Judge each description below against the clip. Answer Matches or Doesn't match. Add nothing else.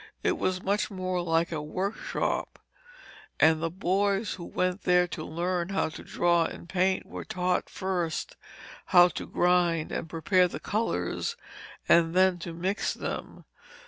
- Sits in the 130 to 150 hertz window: Doesn't match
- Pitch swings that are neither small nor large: Doesn't match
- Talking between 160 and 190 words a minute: Doesn't match